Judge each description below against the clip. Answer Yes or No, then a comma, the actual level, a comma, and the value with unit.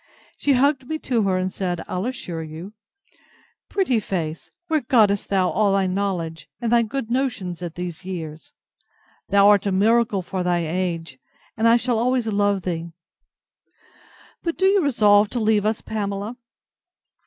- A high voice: Yes, high, 200 Hz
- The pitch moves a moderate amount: Yes, average, 4.7 semitones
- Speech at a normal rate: Yes, average, 155 wpm